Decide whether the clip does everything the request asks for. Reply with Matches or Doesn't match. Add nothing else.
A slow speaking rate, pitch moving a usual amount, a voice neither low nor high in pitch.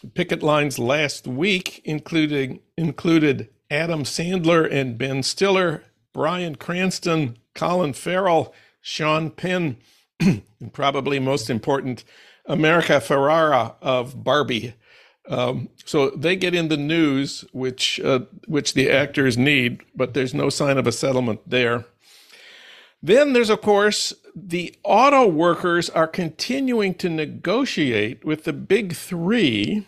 Matches